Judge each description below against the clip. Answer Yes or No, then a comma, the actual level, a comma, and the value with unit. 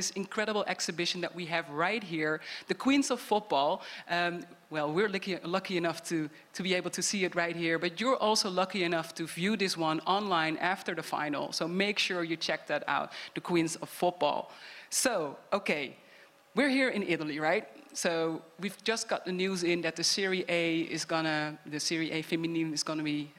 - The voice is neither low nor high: Yes, medium, 175 Hz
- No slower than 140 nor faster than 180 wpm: No, average, 200 wpm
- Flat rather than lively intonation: No, average, 3.1 semitones